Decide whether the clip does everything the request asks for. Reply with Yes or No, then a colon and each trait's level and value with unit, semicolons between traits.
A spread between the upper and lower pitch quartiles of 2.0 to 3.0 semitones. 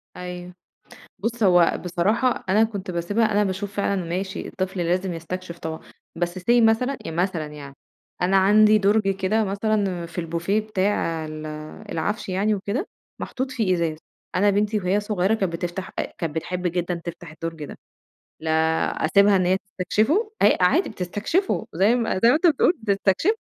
No: average, 3.4 semitones